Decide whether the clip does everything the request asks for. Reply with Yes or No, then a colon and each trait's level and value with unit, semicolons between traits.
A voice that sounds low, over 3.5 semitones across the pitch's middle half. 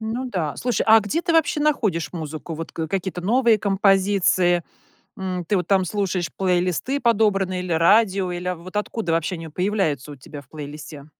No: medium, 185 Hz; average, 4.0 semitones